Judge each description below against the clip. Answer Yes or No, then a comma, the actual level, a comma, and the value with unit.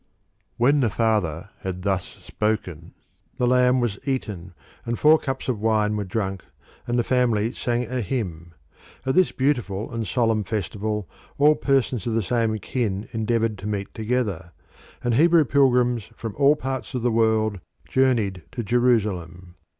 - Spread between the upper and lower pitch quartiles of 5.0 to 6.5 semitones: No, average, 3.8 semitones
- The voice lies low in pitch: Yes, low, 115 Hz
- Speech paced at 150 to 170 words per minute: Yes, average, 155 wpm